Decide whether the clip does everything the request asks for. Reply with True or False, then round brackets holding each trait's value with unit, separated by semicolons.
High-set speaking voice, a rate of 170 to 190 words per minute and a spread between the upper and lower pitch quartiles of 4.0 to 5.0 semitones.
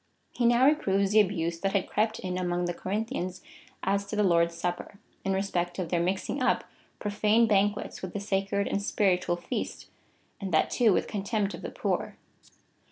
False (195 Hz; 180 wpm; 2.7 semitones)